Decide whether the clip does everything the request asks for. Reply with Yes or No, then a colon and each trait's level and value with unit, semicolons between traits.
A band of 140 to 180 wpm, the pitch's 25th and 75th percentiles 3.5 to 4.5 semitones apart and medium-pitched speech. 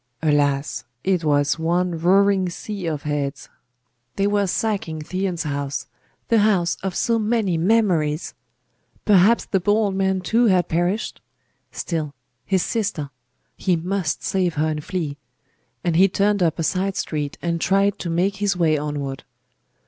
Yes: average, 150 wpm; average, 4.2 semitones; medium, 180 Hz